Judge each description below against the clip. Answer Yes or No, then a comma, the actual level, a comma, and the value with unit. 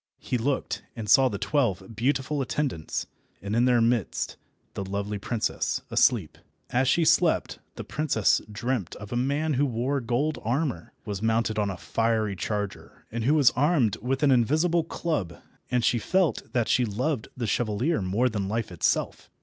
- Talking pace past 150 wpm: Yes, average, 170 wpm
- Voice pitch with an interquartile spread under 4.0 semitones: No, average, 4.8 semitones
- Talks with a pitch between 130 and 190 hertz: No, low, 120 Hz